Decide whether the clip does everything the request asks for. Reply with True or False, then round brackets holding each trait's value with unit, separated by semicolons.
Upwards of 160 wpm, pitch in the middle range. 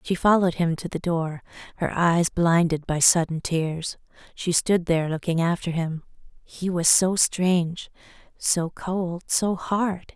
False (155 wpm; 170 Hz)